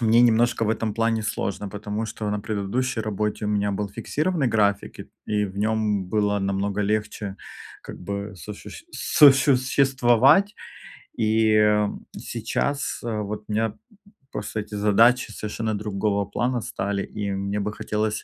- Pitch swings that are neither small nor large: No, narrow, 1.8 semitones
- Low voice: Yes, low, 105 Hz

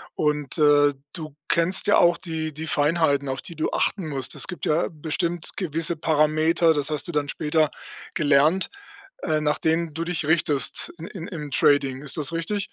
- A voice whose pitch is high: No, medium, 155 Hz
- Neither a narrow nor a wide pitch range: No, narrow, 2.2 semitones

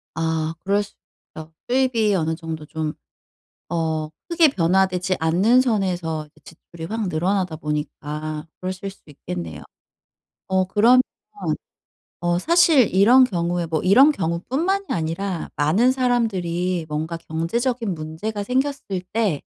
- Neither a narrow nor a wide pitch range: No, wide, 5.7 semitones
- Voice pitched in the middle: Yes, medium, 180 Hz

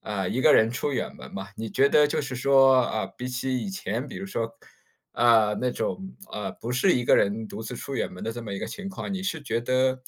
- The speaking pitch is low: Yes, low, 125 Hz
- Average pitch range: Yes, average, 3.7 semitones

